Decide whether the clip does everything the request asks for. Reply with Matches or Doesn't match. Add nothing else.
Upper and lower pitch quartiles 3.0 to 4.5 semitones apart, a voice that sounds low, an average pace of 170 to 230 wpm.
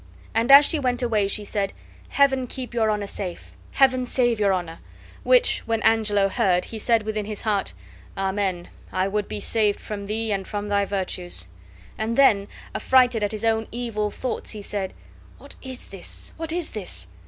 Doesn't match